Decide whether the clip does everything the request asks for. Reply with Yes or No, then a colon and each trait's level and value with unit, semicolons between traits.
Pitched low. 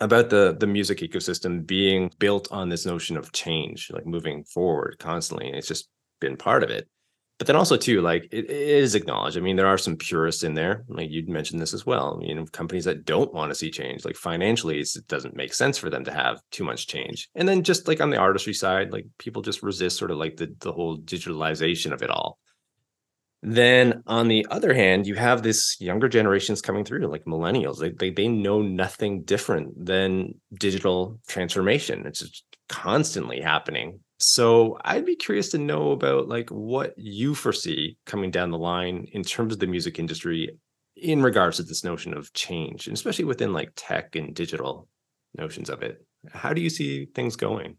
Yes: low, 100 Hz